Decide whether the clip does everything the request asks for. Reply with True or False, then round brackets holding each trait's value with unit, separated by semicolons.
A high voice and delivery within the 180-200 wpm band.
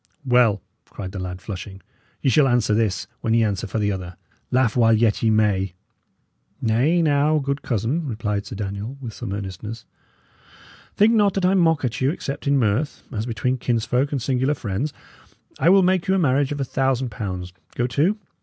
False (120 Hz; 190 wpm)